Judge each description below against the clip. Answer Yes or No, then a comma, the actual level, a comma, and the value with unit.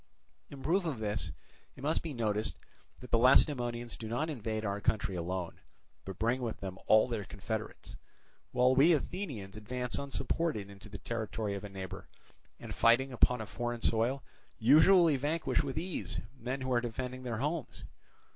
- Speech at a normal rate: Yes, average, 165 wpm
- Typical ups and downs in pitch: Yes, average, 4.2 semitones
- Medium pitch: No, low, 120 Hz